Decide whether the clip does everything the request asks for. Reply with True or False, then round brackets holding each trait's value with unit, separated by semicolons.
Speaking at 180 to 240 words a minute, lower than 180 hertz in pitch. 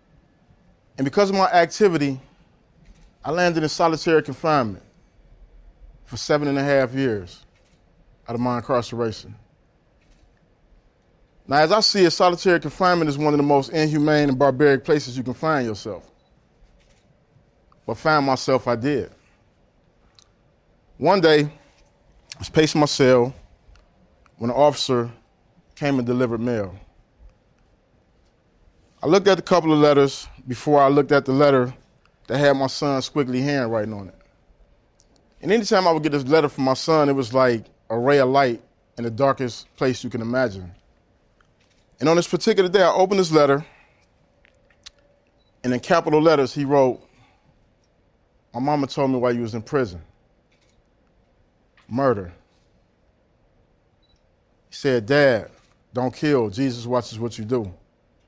False (145 wpm; 135 Hz)